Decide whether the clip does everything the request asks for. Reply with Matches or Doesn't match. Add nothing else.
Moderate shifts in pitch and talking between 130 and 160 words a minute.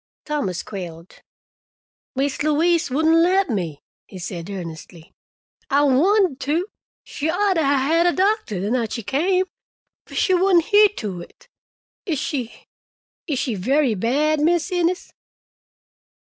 Doesn't match